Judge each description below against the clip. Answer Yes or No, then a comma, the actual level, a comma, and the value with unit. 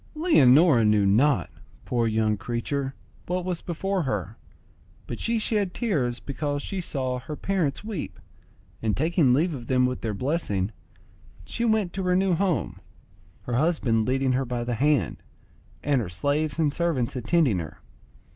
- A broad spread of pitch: Yes, wide, 6.4 semitones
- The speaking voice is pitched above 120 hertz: Yes, medium, 140 Hz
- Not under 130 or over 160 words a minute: Yes, average, 155 wpm